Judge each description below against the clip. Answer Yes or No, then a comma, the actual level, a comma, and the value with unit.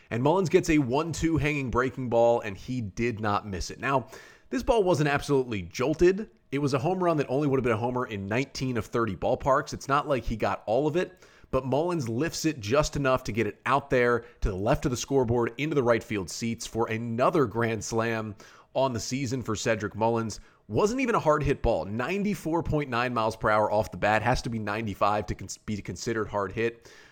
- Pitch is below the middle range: Yes, low, 120 Hz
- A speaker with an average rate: No, fast, 225 wpm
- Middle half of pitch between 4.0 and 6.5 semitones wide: Yes, average, 4.4 semitones